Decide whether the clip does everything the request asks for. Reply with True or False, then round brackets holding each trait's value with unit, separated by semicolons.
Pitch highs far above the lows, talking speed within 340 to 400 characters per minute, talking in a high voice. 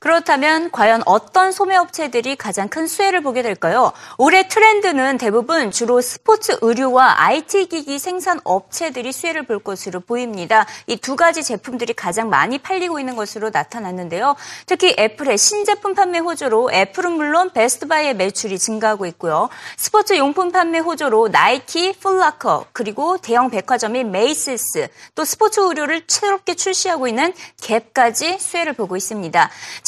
True (8.3 semitones; 360 characters per minute; 295 Hz)